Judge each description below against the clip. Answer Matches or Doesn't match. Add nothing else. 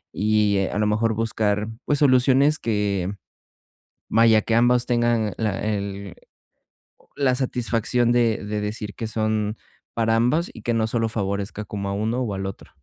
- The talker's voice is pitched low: Matches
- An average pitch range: Doesn't match